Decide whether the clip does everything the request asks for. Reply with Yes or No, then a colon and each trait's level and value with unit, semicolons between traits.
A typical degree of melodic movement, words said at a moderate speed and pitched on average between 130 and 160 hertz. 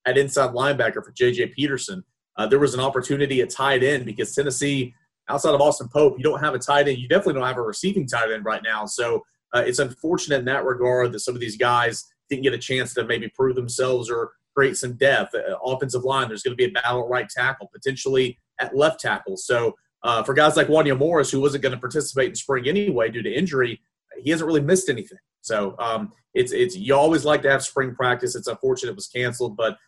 No: average, 3.5 semitones; fast, 235 wpm; low, 135 Hz